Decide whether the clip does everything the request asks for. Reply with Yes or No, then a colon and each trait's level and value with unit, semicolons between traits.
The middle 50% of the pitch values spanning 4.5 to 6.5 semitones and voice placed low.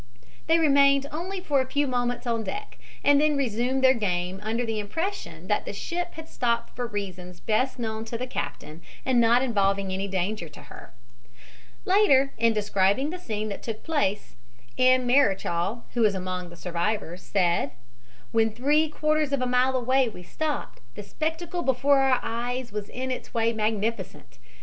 No: average, 5.1 semitones; high, 240 Hz